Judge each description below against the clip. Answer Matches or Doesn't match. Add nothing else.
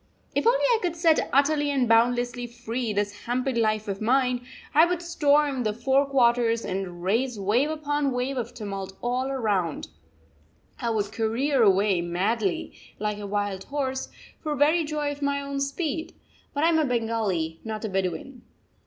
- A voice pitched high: Matches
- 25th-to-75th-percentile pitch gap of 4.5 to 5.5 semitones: Matches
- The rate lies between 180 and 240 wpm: Doesn't match